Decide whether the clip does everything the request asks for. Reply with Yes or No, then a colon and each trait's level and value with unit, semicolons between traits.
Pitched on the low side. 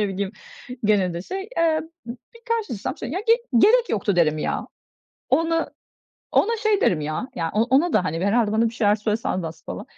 No: high, 220 Hz